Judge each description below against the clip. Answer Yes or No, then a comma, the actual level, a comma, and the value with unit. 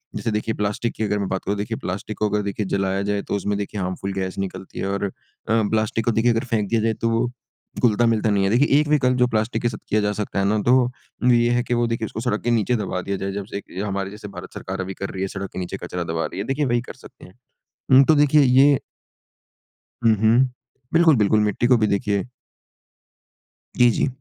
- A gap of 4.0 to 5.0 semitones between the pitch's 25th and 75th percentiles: No, average, 3.3 semitones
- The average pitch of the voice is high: No, low, 105 Hz